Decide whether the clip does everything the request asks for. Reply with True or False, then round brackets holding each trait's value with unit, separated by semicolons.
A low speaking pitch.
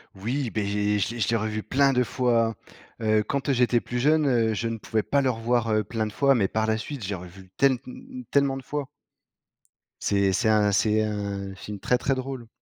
True (115 Hz)